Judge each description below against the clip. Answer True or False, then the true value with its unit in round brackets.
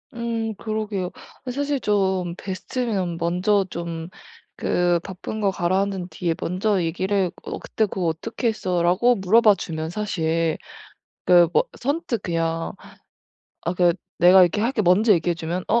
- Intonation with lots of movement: False (3.8 semitones)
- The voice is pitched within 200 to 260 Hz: False (185 Hz)